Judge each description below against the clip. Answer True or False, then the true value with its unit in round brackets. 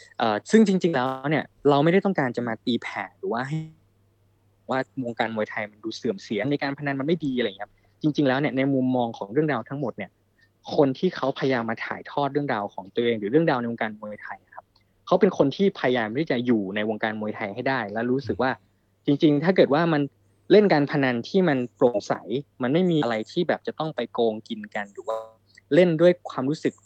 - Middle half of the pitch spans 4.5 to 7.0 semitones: True (5.2 semitones)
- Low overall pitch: True (130 Hz)